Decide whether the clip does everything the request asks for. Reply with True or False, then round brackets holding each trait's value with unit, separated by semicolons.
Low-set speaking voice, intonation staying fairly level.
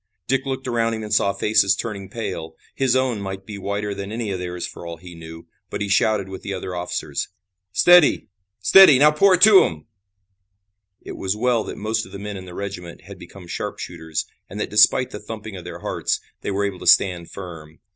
False (100 Hz; 3.9 semitones)